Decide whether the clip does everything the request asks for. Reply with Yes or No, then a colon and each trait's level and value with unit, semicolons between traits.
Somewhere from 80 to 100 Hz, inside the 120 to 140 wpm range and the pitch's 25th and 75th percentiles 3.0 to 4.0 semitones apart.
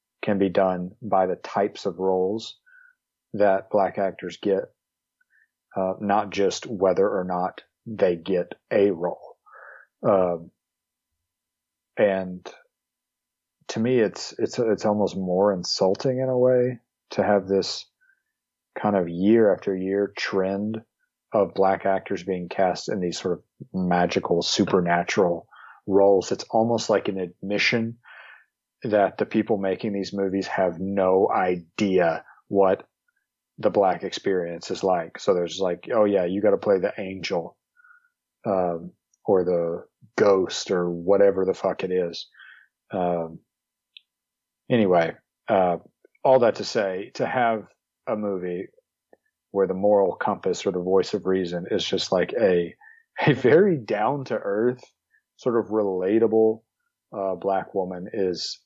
Yes: very low, 95 Hz; slow, 135 wpm; average, 3.4 semitones